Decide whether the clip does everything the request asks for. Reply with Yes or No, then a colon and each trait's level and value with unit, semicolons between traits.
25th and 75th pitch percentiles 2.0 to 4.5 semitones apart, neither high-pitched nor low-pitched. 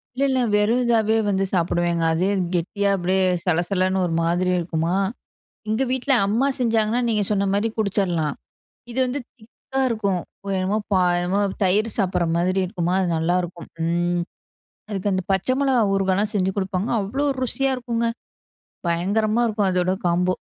No: average, 3.7 semitones; high, 195 Hz